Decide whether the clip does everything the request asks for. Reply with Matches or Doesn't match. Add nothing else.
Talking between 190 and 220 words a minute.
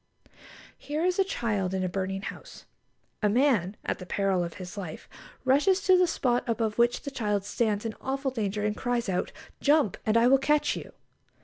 Matches